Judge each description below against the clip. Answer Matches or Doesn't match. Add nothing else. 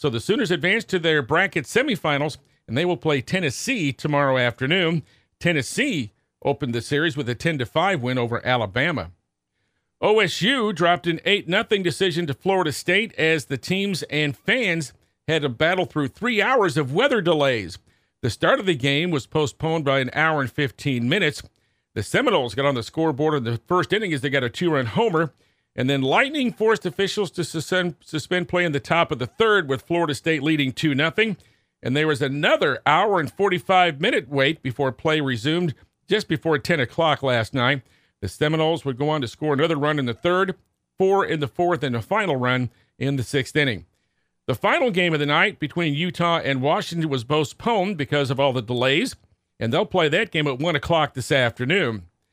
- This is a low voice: Doesn't match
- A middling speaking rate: Matches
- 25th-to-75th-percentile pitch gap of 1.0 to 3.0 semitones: Doesn't match